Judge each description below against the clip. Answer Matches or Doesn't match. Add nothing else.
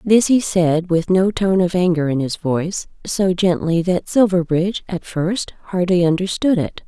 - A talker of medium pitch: Matches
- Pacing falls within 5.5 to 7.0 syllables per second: Doesn't match